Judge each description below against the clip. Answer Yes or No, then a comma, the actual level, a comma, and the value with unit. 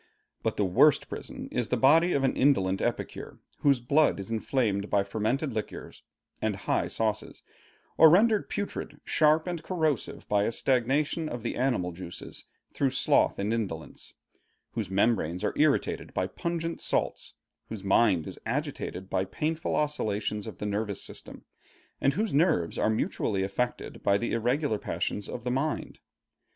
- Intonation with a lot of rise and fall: Yes, wide, 6.8 semitones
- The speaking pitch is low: Yes, low, 120 Hz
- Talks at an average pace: Yes, average, 155 wpm